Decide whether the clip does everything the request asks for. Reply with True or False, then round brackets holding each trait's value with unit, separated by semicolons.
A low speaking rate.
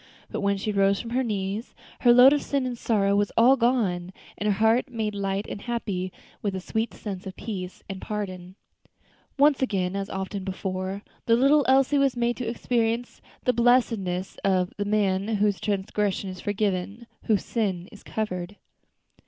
False (175 wpm)